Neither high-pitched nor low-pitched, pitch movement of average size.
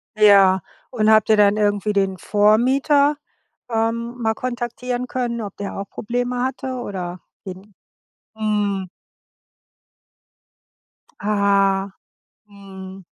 No: high, 210 Hz; average, 3.3 semitones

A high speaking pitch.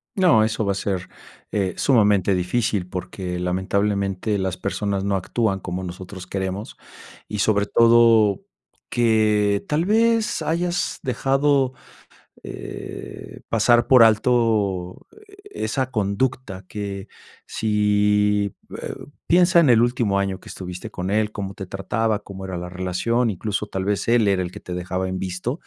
No: low, 105 Hz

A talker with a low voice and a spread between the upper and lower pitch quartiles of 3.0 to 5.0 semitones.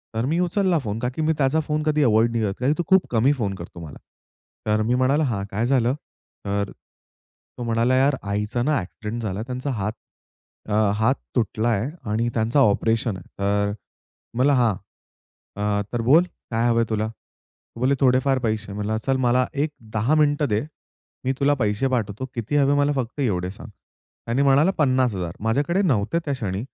Yes: low, 120 Hz; average, 4.5 semitones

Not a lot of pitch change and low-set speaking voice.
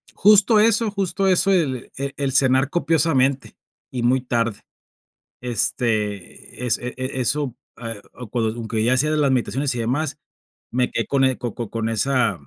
No: average, 3.8 semitones; low, 130 Hz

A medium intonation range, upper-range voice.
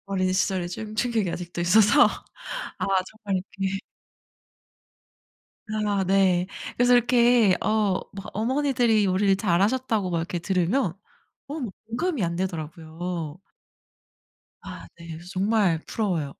Yes: average, 4.1 semitones; high, 195 Hz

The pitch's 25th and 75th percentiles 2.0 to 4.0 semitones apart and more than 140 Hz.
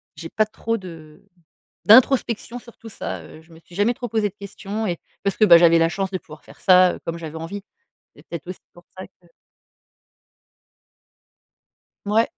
No: average, 4.4 semitones; high, 190 Hz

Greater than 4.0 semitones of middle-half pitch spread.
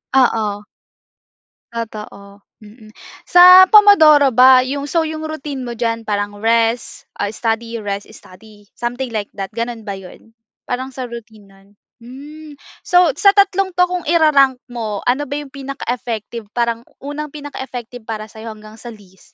Yes: average, 4.9 semitones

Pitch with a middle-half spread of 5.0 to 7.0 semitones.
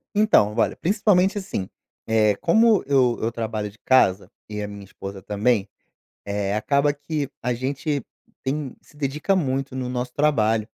Yes: wide, 5.6 semitones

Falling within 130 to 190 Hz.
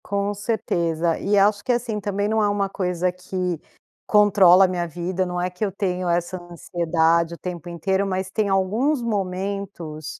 Yes: medium, 185 Hz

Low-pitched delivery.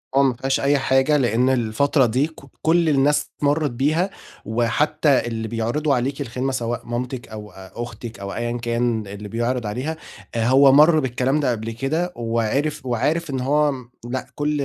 Yes: low, 130 Hz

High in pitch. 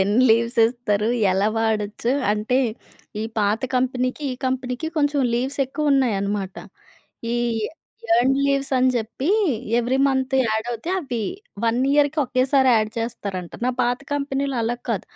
Yes: high, 245 Hz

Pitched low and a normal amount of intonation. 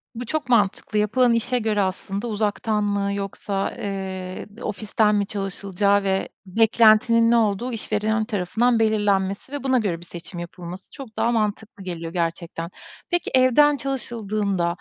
No: high, 210 Hz; average, 3.1 semitones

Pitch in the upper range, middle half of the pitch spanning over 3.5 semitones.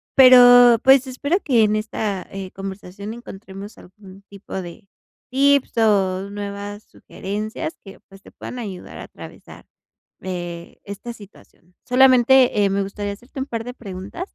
Yes: high, 210 Hz; average, 4.0 semitones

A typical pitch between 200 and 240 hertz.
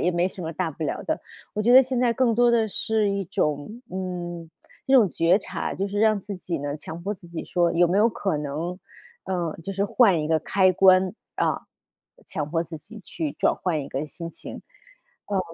No: medium, 185 Hz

